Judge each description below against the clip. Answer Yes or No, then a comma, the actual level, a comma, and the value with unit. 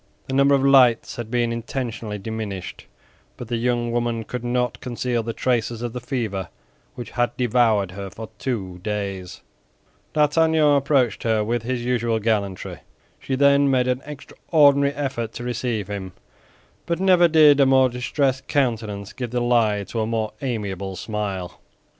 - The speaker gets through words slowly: No, average, 160 wpm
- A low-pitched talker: Yes, low, 120 Hz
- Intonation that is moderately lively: Yes, average, 3.4 semitones